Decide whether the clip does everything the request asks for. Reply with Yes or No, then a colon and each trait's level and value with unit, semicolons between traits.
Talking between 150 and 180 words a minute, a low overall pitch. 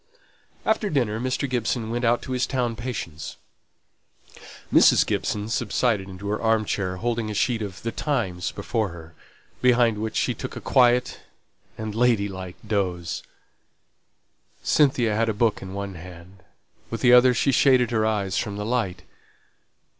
Yes: average, 155 wpm; low, 110 Hz